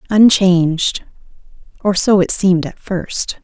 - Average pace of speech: No, slow, 105 wpm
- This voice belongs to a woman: Yes, female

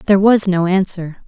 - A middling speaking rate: Yes, average, 190 wpm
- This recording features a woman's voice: Yes, female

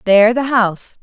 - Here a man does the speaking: No, female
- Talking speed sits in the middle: Yes, average, 175 wpm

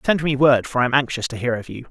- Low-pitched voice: Yes, low, 130 Hz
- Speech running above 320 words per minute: Yes, fast, 345 wpm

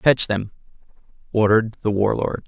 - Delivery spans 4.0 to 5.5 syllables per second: Yes, 4.9 syllables/s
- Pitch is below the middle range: Yes, low, 110 Hz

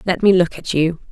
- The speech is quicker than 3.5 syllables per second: Yes, 5.6 syllables/s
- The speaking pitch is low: No, medium, 175 Hz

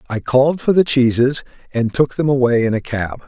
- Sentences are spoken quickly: Yes, fast, 220 wpm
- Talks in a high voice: No, low, 130 Hz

